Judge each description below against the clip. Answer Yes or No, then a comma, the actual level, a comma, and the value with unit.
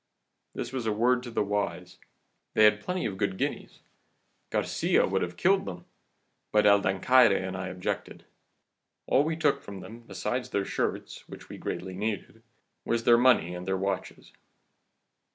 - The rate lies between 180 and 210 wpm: No, average, 165 wpm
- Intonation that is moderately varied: Yes, average, 4.4 semitones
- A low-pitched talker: Yes, low, 105 Hz